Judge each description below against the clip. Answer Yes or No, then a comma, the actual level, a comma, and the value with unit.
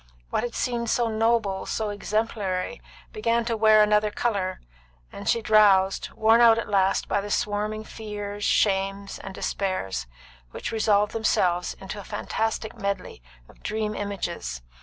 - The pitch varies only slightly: Yes, narrow, 2.1 semitones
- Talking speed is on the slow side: No, average, 145 wpm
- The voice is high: Yes, high, 210 Hz